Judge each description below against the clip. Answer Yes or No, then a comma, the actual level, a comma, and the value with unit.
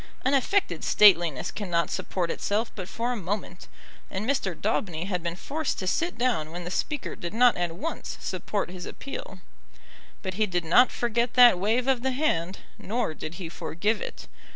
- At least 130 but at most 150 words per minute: No, average, 180 wpm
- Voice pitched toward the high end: Yes, high, 205 Hz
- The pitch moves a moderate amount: No, wide, 5.8 semitones